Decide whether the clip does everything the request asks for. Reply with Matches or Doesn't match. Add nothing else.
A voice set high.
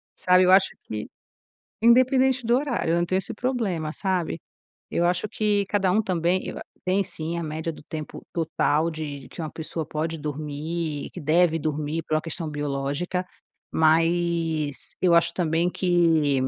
Doesn't match